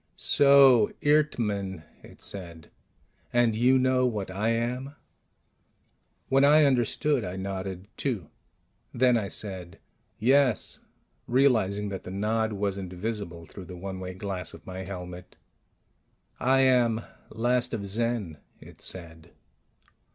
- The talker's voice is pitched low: Yes, low, 105 Hz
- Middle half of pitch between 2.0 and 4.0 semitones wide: No, average, 4.9 semitones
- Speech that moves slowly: Yes, slow, 125 wpm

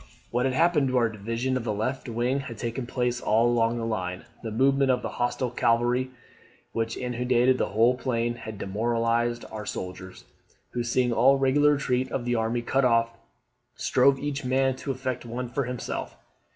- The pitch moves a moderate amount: No, narrow, 2.1 semitones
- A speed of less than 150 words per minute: No, average, 180 wpm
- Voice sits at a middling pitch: No, low, 120 Hz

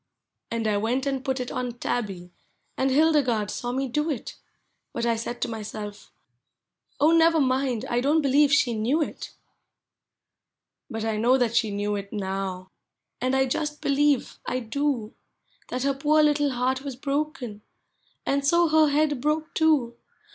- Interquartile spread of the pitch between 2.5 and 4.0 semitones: No, average, 4.4 semitones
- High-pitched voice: Yes, very high, 260 Hz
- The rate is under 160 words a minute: No, average, 170 wpm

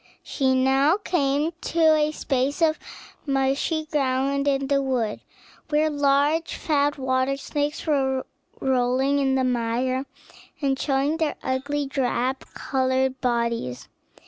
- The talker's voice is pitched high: Yes, very high, 275 Hz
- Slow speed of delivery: Yes, slow, 120 wpm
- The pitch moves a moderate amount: No, narrow, 2.0 semitones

